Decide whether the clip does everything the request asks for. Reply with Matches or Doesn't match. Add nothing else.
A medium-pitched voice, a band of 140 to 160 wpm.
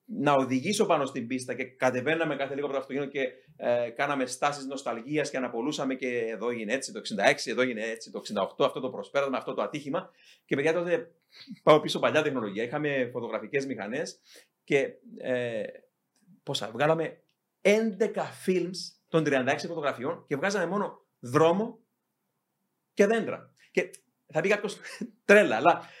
Matches